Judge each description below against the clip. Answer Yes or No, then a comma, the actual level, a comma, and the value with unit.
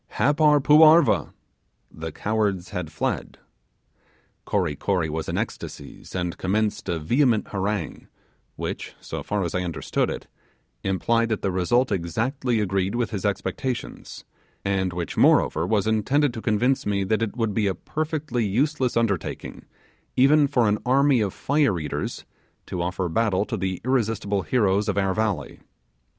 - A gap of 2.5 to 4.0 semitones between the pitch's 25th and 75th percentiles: No, average, 4.8 semitones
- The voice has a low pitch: Yes, low, 105 Hz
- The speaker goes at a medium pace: Yes, average, 150 wpm